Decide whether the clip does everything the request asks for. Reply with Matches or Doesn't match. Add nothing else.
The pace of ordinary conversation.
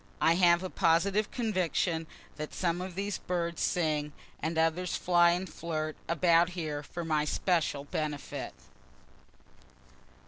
Doesn't match